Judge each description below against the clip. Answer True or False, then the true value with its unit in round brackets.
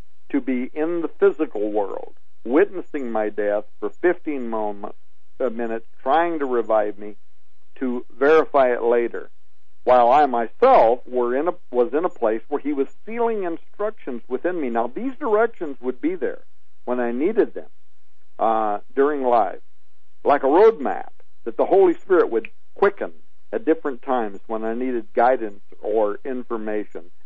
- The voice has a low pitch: True (130 Hz)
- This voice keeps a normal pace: True (150 wpm)